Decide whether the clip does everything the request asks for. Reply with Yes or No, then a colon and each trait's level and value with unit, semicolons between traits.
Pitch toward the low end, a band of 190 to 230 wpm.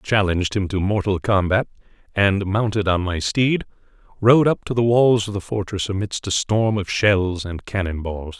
Yes: low, 100 Hz; average, 195 wpm